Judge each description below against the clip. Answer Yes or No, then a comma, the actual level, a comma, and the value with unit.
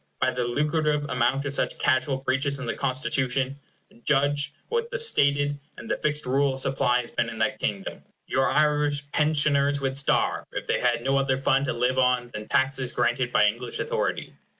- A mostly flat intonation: Yes, narrow, 2.1 semitones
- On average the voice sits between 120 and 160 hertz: Yes, low, 135 Hz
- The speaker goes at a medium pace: Yes, average, 185 wpm